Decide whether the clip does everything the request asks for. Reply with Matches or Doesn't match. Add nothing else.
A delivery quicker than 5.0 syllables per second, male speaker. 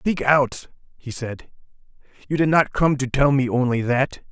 Doesn't match